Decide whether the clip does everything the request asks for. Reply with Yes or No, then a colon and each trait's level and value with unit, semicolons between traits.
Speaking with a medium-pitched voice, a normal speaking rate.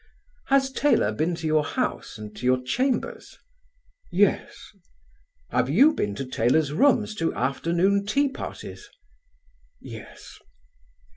No: medium, 165 Hz; slow, 120 wpm